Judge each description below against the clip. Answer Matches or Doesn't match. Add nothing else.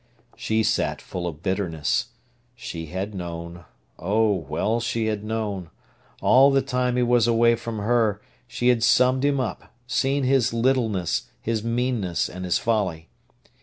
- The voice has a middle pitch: Doesn't match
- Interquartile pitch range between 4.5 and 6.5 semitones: Matches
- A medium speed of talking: Matches